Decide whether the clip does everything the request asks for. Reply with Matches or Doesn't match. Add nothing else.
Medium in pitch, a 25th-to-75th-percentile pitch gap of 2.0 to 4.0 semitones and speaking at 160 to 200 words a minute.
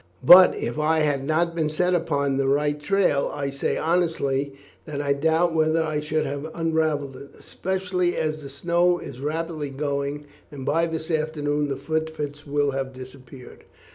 Matches